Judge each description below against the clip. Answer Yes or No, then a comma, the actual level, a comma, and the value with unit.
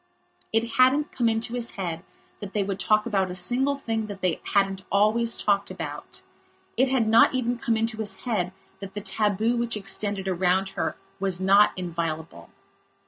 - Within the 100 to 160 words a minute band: No, average, 175 wpm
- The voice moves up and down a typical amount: Yes, average, 3.3 semitones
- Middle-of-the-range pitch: No, high, 210 Hz